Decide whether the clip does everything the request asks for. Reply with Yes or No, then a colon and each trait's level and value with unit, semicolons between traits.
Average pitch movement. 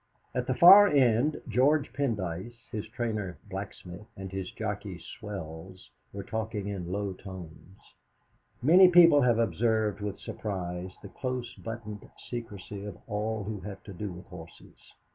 Yes: average, 3.8 semitones